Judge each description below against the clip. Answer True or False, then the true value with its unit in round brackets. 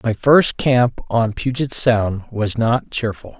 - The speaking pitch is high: False (115 Hz)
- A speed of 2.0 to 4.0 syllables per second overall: True (3.5 syllables/s)